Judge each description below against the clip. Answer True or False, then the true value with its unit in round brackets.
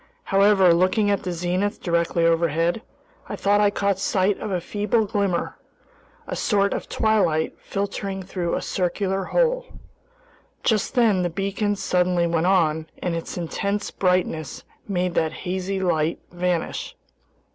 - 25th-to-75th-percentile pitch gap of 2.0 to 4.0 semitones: True (2.7 semitones)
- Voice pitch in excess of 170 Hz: True (185 Hz)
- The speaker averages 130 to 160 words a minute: True (140 wpm)